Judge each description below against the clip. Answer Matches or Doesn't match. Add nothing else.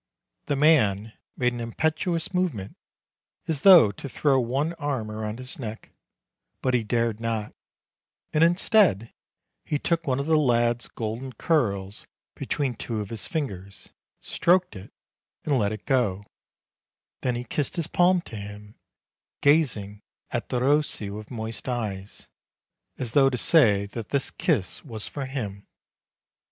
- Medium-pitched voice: Doesn't match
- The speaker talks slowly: Doesn't match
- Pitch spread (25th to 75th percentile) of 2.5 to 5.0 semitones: Doesn't match